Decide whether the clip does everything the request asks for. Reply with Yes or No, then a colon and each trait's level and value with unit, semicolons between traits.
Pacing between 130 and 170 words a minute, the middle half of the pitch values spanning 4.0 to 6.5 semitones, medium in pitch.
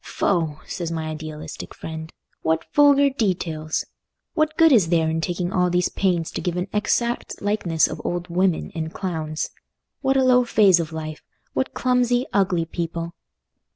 Yes: average, 160 wpm; average, 5.2 semitones; medium, 175 Hz